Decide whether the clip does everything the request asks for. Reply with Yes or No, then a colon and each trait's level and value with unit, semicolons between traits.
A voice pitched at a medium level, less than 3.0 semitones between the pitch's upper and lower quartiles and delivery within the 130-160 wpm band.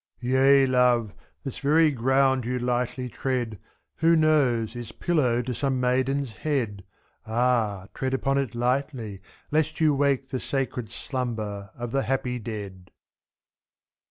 No: low, 125 Hz; narrow, 2.6 semitones; slow, 135 wpm